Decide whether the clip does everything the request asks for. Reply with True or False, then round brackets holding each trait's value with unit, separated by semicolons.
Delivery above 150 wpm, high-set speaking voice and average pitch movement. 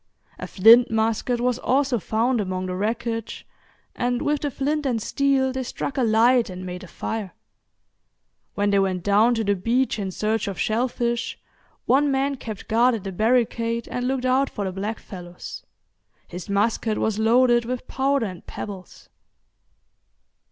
True (160 wpm; 230 Hz; 3.8 semitones)